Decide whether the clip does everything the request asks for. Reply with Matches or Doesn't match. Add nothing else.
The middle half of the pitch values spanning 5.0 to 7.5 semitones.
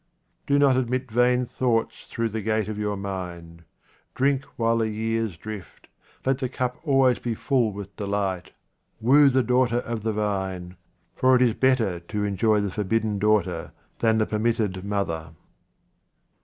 Doesn't match